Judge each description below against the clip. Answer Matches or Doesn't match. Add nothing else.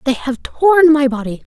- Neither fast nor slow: Matches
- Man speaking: Doesn't match